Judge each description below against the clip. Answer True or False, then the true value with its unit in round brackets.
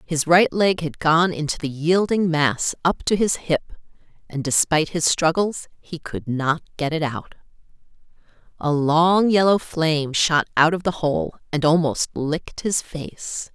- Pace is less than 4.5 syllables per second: True (4.2 syllables/s)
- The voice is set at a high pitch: False (160 Hz)